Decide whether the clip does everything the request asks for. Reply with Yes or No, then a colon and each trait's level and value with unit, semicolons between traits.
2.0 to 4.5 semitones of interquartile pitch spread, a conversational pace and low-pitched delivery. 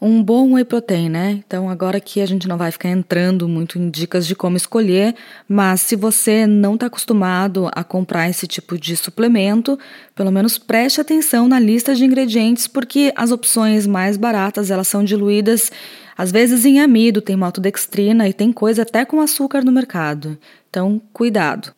No: average, 4.0 semitones; average, 175 wpm; high, 210 Hz